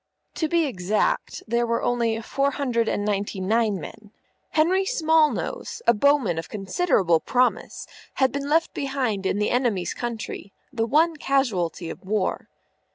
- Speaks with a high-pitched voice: Yes, high, 235 Hz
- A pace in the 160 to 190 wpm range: No, average, 150 wpm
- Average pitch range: No, wide, 5.7 semitones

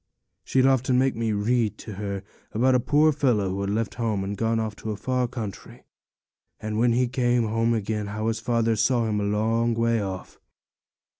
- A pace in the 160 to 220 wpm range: Yes, average, 195 wpm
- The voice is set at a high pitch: No, low, 115 Hz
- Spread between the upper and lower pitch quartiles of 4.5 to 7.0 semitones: No, narrow, 2.6 semitones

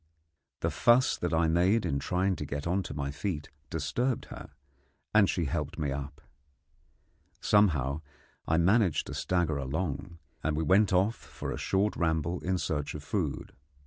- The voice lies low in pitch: Yes, very low, 85 Hz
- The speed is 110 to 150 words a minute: No, average, 165 wpm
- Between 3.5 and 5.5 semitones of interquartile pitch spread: Yes, average, 4.3 semitones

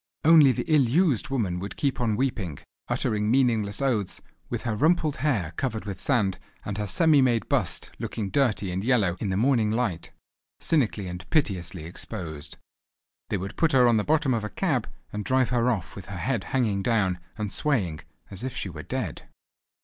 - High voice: No, low, 110 Hz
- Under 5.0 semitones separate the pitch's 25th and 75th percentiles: No, average, 5.3 semitones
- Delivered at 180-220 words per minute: Yes, average, 190 wpm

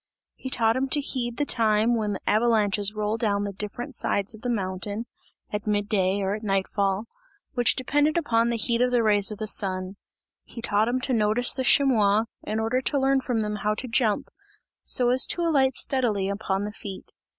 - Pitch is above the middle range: Yes, high, 220 Hz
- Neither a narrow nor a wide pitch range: Yes, average, 3.3 semitones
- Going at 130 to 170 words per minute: No, fast, 205 wpm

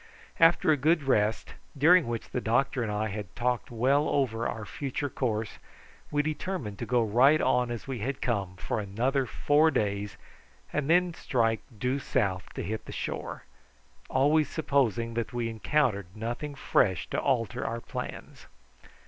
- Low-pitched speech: Yes, low, 120 Hz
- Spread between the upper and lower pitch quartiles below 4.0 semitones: No, average, 4.4 semitones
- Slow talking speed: No, average, 165 wpm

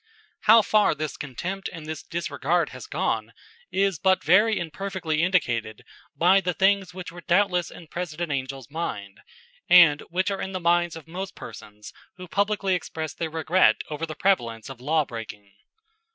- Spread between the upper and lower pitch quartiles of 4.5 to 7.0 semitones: No, average, 3.9 semitones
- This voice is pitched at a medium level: Yes, medium, 170 Hz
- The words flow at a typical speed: Yes, average, 165 wpm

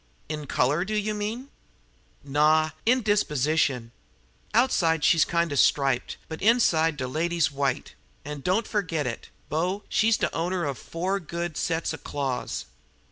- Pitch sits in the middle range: Yes, medium, 160 Hz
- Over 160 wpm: No, average, 150 wpm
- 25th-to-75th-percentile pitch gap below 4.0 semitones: No, average, 5.0 semitones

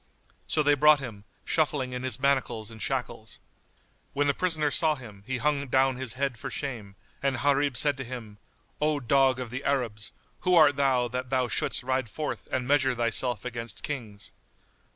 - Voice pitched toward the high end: No, low, 130 Hz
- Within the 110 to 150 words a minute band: No, average, 180 wpm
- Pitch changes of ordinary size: Yes, average, 3.0 semitones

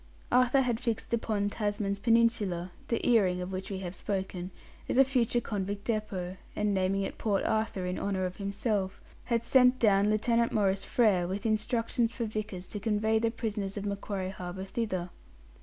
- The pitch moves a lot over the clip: No, average, 3.2 semitones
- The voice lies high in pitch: Yes, high, 205 Hz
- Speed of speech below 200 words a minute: Yes, average, 175 wpm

